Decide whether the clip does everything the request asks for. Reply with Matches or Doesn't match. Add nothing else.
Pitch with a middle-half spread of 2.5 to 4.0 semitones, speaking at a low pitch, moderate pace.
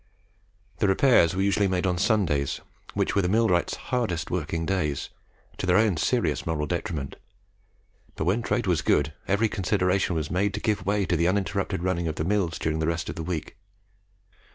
Matches